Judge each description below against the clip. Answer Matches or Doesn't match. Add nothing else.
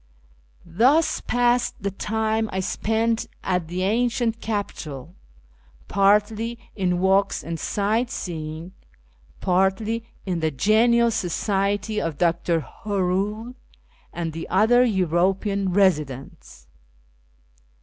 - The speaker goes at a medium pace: Doesn't match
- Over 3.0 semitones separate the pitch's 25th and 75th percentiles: Matches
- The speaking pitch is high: Matches